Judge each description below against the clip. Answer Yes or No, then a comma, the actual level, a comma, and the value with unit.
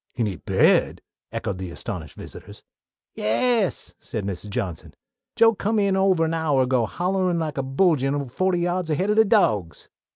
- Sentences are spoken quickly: No, average, 165 wpm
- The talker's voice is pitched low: No, medium, 160 Hz